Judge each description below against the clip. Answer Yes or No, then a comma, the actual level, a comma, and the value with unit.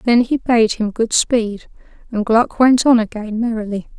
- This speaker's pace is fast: No, average, 180 wpm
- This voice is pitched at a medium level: No, high, 225 Hz